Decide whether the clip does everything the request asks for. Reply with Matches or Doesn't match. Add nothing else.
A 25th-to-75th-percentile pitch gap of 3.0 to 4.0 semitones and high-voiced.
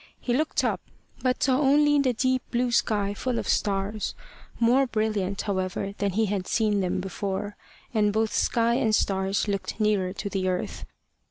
Matches